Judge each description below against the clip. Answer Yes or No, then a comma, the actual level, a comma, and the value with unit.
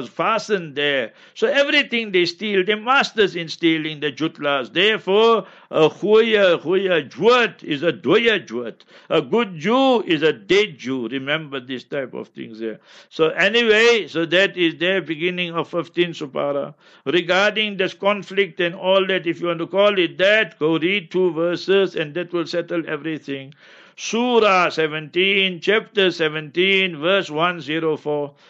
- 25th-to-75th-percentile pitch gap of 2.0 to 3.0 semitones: No, average, 4.2 semitones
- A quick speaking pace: No, average, 160 wpm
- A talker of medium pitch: Yes, medium, 175 Hz